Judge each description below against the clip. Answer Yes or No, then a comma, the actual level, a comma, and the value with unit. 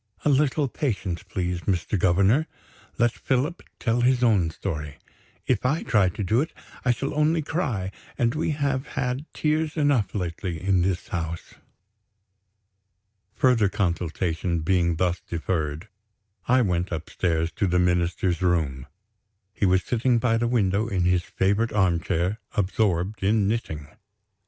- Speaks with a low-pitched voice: Yes, low, 100 Hz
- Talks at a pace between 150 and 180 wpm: No, average, 140 wpm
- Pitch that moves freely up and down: Yes, wide, 6.0 semitones